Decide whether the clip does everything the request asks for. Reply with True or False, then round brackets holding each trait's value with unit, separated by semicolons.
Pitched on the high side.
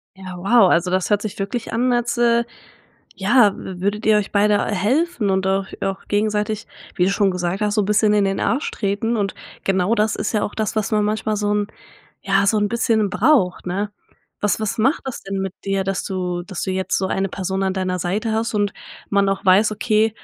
True (205 Hz)